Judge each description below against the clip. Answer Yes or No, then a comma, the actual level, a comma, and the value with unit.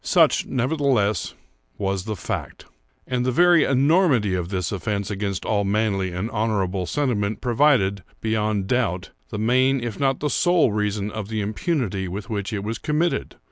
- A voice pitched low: Yes, low, 110 Hz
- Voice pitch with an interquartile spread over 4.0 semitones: Yes, average, 4.5 semitones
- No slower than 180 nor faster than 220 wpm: No, average, 160 wpm